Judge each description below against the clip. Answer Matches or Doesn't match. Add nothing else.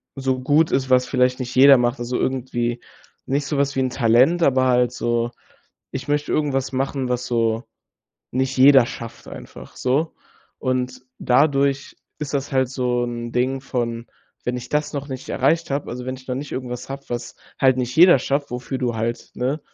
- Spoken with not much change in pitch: Matches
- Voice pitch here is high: Doesn't match